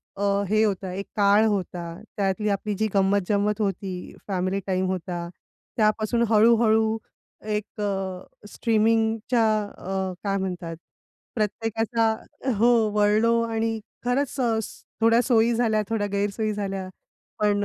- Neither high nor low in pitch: No, high, 210 Hz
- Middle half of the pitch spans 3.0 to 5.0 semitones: No, narrow, 2.5 semitones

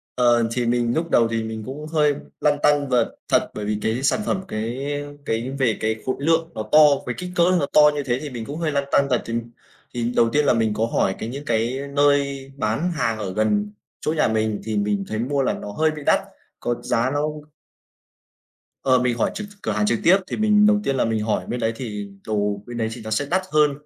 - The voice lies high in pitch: No, low, 120 Hz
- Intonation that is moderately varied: Yes, average, 4.7 semitones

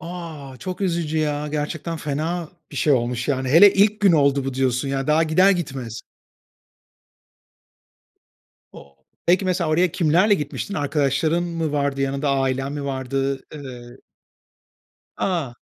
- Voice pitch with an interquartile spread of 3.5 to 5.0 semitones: Yes, average, 3.9 semitones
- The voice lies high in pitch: No, medium, 150 Hz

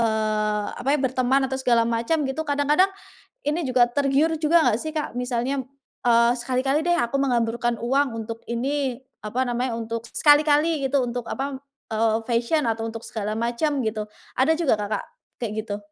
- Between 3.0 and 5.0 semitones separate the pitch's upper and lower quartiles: Yes, average, 3.7 semitones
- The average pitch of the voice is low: No, very high, 250 Hz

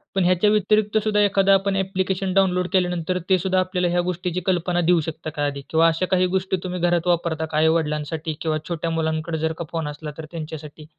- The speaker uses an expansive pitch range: No, average, 2.7 semitones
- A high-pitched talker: No, medium, 175 Hz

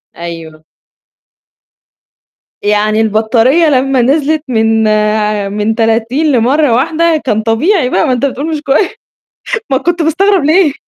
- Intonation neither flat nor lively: No, wide, 6.0 semitones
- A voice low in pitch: No, very high, 250 Hz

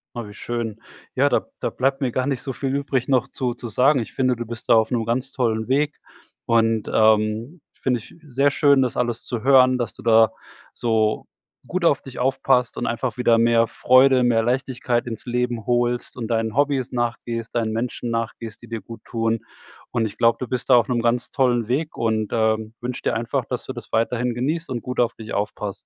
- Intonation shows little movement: Yes, narrow, 2.2 semitones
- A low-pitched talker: Yes, low, 120 Hz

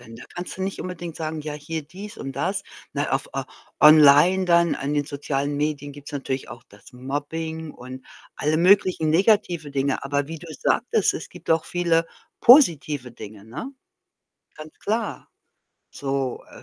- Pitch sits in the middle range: Yes, medium, 150 Hz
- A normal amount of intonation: Yes, average, 3.5 semitones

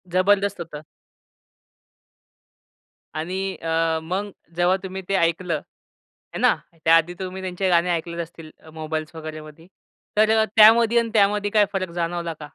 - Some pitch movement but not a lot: Yes, average, 3.3 semitones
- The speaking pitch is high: No, medium, 175 Hz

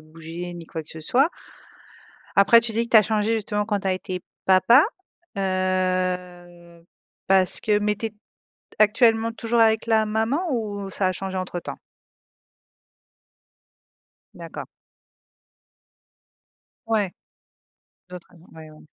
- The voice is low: No, high, 195 Hz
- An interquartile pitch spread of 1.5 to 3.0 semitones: No, average, 3.6 semitones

